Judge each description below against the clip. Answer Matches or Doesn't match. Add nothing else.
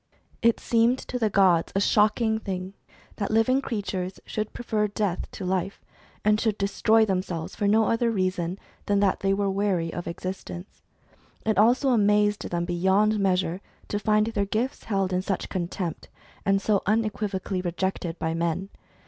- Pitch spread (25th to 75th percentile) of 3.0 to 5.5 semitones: Doesn't match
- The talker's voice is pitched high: Matches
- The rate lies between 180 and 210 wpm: Doesn't match